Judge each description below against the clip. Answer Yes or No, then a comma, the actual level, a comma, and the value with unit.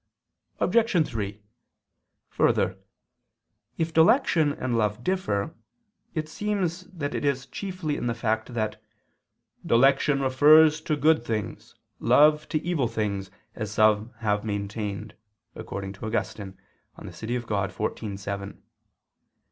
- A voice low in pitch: Yes, low, 120 Hz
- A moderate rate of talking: No, slow, 120 wpm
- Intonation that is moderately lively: No, wide, 6.6 semitones